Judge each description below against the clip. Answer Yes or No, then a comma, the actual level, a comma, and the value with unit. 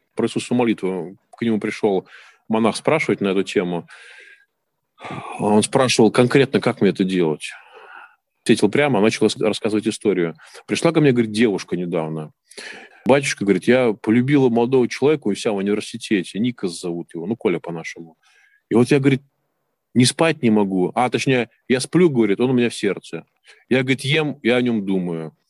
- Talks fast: Yes, fast, 165 wpm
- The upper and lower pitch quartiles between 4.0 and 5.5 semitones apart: Yes, average, 4.9 semitones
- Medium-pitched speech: No, low, 115 Hz